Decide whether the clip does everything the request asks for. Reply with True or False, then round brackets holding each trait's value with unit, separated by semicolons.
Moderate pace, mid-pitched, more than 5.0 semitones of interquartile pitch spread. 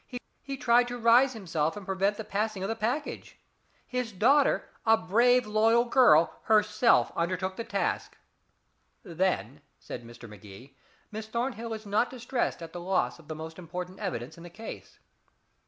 False (160 wpm; 210 Hz; 5.4 semitones)